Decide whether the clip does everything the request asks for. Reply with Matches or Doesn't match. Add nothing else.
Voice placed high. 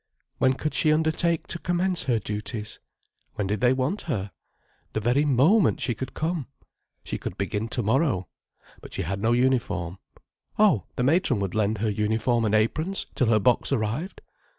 Doesn't match